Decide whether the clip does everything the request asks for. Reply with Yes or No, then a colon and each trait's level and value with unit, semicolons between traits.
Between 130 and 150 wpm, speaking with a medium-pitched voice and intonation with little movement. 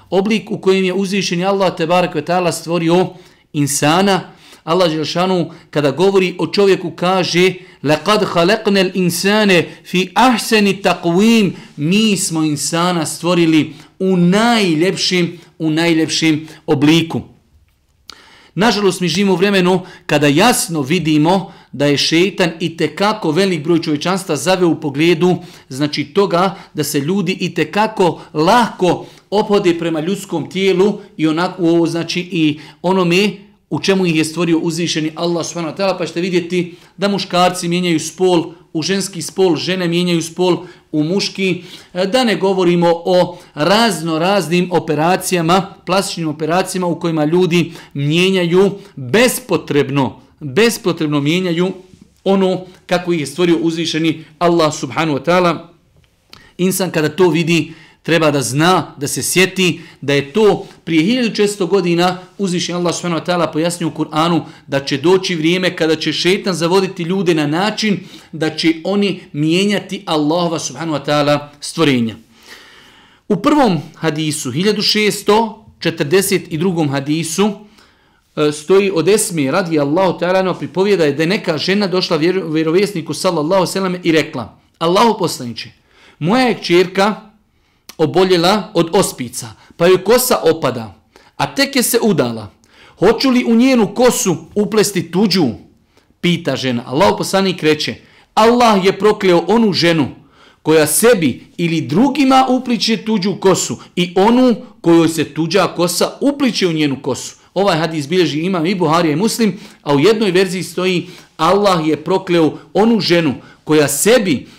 No: average, 140 wpm; medium, 175 Hz; average, 3.3 semitones